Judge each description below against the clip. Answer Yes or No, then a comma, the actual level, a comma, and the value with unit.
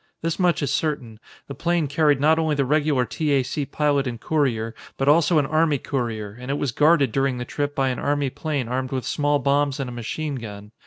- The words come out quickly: Yes, fast, 225 wpm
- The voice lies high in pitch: No, medium, 140 Hz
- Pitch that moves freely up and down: No, average, 3.1 semitones